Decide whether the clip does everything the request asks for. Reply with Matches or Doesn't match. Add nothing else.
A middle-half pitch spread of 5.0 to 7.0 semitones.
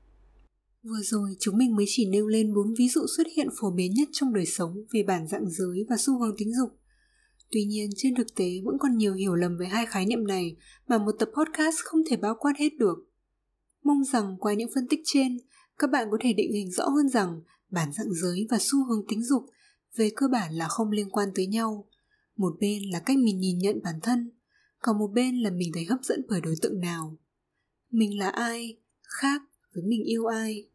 Doesn't match